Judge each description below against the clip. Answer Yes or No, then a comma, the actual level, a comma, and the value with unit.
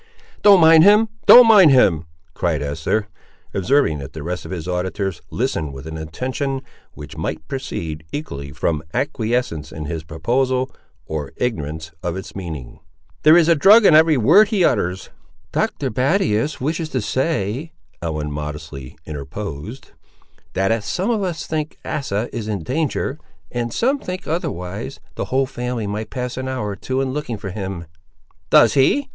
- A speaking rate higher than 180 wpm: No, average, 165 wpm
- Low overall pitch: Yes, low, 115 Hz